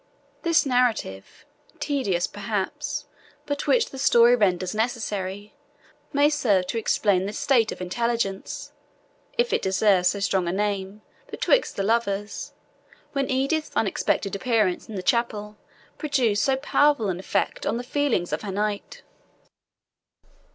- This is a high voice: Yes, high, 215 Hz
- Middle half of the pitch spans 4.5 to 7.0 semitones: Yes, average, 5.3 semitones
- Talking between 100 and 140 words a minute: Yes, slow, 135 wpm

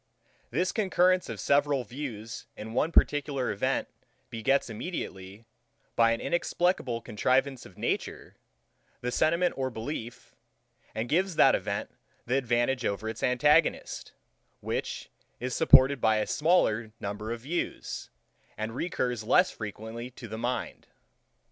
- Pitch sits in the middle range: No, low, 125 Hz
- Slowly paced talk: Yes, slow, 130 wpm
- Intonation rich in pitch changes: No, average, 4.7 semitones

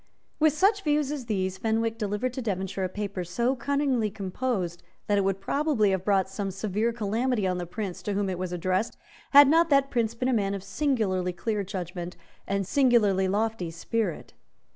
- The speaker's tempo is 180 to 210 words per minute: Yes, average, 185 wpm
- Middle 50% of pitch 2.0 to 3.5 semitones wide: No, average, 4.6 semitones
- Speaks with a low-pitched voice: No, high, 210 Hz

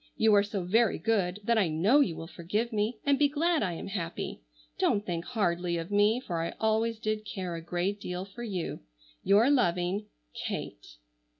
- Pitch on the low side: No, high, 205 Hz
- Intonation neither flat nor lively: Yes, average, 4.2 semitones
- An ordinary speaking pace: Yes, average, 190 wpm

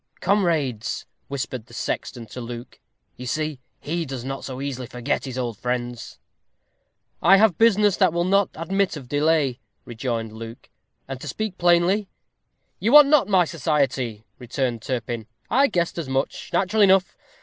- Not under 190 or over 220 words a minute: No, average, 160 wpm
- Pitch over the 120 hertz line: Yes, medium, 140 Hz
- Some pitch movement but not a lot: No, wide, 7.2 semitones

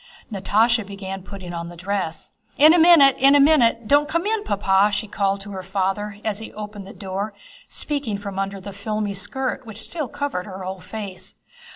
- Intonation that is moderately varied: Yes, average, 3.8 semitones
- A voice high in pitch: Yes, high, 205 Hz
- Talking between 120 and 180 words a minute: No, average, 190 wpm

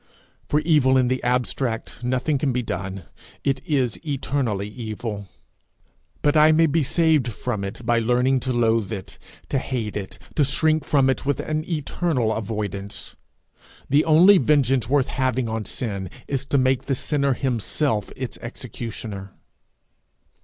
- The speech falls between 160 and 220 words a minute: No, average, 150 wpm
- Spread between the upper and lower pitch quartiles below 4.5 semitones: Yes, average, 4.1 semitones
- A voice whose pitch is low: Yes, low, 130 Hz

